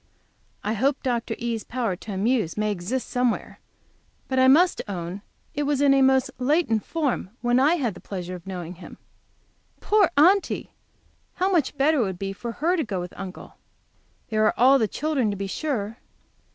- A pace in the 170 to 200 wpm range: Yes, average, 180 wpm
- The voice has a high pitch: Yes, high, 240 Hz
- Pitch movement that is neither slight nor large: No, wide, 5.9 semitones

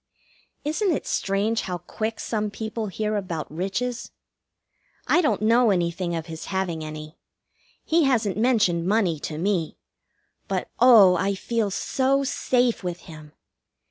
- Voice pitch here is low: No, high, 200 Hz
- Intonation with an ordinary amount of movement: Yes, average, 5.0 semitones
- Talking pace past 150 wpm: No, average, 140 wpm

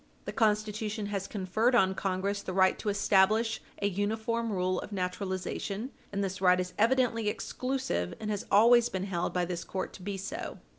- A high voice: Yes, high, 200 Hz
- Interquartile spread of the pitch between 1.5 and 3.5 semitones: Yes, average, 2.8 semitones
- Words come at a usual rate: Yes, average, 180 wpm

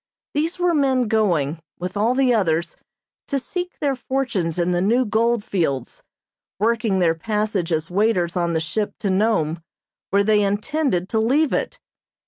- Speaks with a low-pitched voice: No, high, 210 Hz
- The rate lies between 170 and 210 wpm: No, average, 160 wpm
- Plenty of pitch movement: Yes, wide, 6.1 semitones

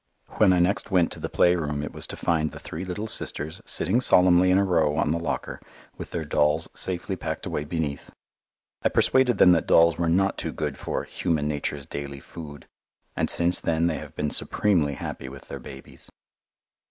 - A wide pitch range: No, average, 3.4 semitones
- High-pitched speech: No, very low, 85 Hz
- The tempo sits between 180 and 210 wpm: Yes, average, 195 wpm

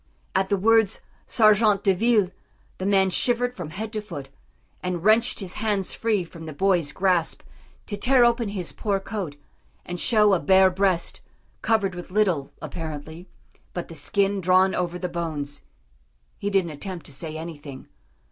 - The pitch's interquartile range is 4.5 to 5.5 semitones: No, average, 3.8 semitones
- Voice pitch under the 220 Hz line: Yes, high, 190 Hz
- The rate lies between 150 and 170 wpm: Yes, average, 165 wpm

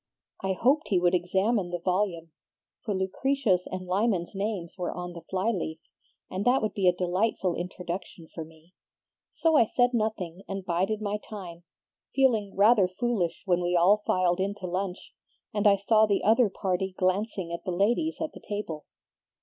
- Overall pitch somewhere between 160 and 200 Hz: Yes, high, 190 Hz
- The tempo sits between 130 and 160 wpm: No, average, 175 wpm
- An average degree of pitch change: Yes, average, 3.2 semitones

